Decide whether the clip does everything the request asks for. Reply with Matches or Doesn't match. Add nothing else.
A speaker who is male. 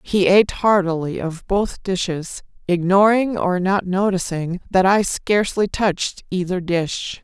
Doesn't match